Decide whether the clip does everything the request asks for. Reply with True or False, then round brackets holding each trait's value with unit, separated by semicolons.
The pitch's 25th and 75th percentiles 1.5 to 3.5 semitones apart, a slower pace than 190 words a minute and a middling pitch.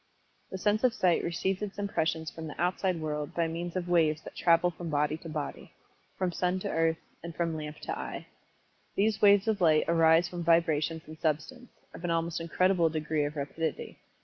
False (2.4 semitones; 195 wpm; 165 Hz)